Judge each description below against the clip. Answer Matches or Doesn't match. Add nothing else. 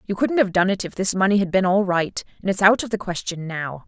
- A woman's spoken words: Matches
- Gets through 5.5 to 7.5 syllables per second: Matches